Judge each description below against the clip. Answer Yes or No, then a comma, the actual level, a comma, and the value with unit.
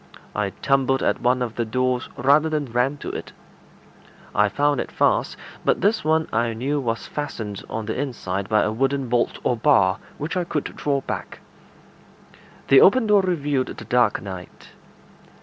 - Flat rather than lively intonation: No, average, 4.5 semitones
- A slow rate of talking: No, average, 170 wpm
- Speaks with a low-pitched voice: Yes, low, 130 Hz